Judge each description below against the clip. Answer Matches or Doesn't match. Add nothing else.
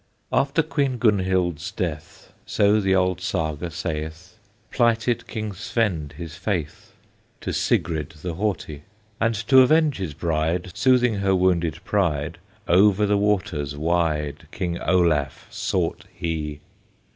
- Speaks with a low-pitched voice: Matches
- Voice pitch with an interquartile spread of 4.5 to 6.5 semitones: Matches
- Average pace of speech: Doesn't match